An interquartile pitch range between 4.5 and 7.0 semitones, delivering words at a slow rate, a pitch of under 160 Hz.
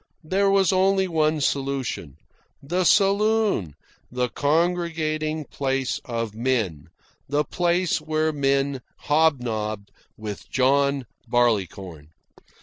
Yes: wide, 5.6 semitones; slow, 95 wpm; medium, 140 Hz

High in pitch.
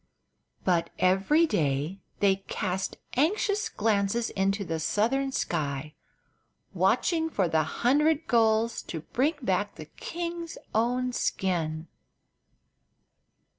Yes: high, 205 Hz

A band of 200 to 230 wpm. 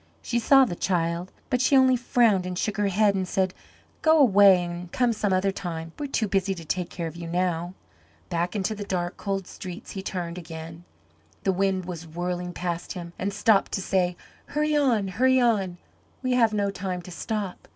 Yes: fast, 205 wpm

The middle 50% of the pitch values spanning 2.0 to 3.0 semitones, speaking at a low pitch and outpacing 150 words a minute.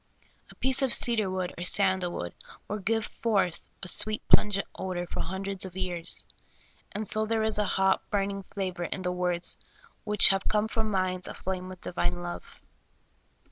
No: average, 2.7 semitones; high, 190 Hz; average, 175 wpm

